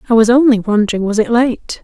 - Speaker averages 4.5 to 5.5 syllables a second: No, 6.1 syllables/s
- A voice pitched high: Yes, high, 230 Hz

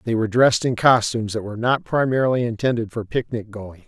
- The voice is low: Yes, low, 115 Hz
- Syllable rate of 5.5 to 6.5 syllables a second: Yes, 6.4 syllables/s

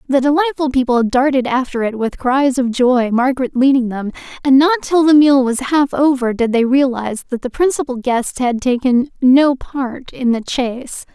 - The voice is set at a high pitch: Yes, very high, 260 Hz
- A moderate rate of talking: Yes, average, 190 wpm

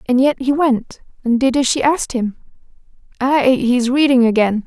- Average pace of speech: Yes, average, 195 wpm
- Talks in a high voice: Yes, very high, 255 Hz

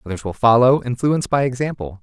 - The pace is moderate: Yes, average, 180 wpm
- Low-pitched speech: Yes, low, 120 Hz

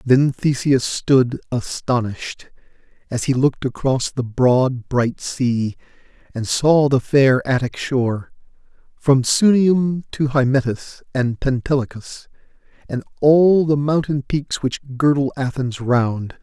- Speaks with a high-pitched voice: No, low, 130 Hz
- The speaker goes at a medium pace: No, slow, 120 wpm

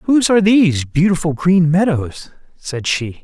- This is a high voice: No, medium, 170 Hz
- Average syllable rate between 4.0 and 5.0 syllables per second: Yes, 4.8 syllables/s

